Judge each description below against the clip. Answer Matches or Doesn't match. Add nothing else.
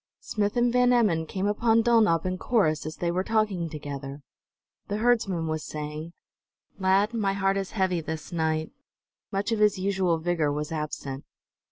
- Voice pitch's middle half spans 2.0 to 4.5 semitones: Doesn't match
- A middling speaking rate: Matches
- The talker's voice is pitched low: Doesn't match